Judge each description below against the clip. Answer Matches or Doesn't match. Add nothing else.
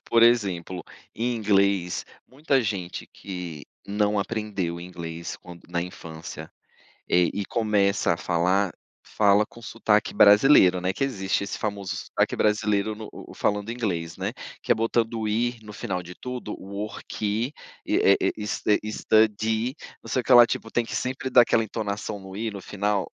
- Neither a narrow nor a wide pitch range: Matches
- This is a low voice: Matches